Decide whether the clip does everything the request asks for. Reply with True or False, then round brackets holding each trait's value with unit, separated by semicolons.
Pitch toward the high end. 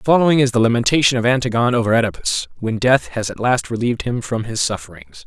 False (120 Hz)